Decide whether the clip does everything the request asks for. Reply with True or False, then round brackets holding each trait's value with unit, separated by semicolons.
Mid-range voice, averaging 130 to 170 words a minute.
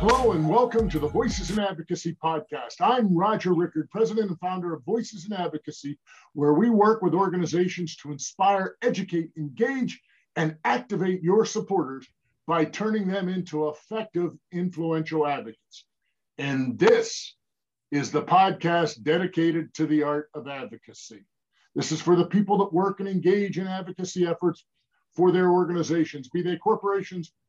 True (175 Hz; 150 wpm)